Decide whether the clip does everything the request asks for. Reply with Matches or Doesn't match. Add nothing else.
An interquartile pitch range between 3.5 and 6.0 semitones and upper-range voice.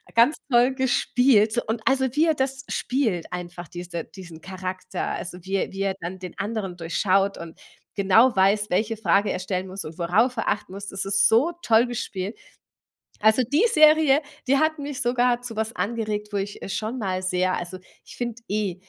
Matches